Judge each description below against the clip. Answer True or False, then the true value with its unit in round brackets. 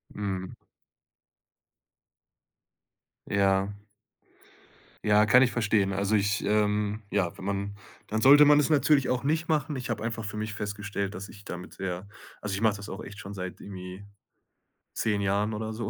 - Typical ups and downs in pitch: False (2.1 semitones)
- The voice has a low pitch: True (105 Hz)